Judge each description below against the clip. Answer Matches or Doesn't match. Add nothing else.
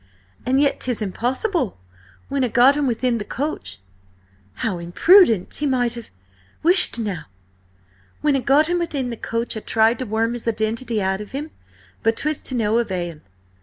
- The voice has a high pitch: Matches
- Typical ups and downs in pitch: Matches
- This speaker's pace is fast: Doesn't match